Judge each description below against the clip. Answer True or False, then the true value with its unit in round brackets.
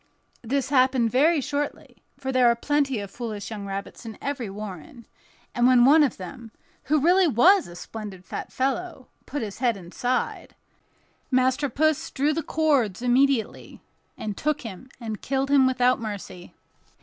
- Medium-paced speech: True (160 wpm)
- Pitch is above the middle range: True (255 Hz)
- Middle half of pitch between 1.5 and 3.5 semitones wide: False (4.4 semitones)